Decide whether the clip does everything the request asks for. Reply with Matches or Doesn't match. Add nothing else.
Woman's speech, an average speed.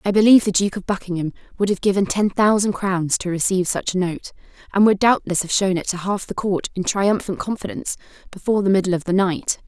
Doesn't match